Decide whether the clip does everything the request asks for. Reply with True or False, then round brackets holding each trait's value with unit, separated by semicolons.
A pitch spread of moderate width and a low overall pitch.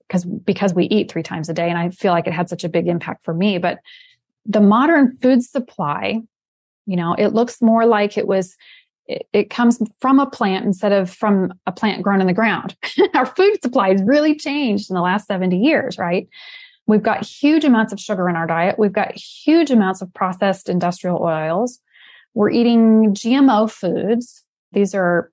False (5.0 semitones; 210 Hz)